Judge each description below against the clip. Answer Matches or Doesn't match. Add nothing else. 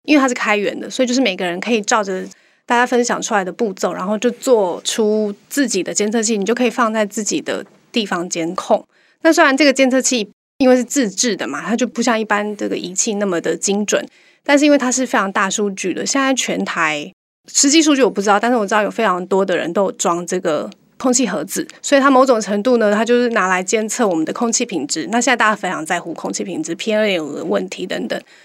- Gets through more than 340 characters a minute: Matches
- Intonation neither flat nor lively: Matches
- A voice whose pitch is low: Doesn't match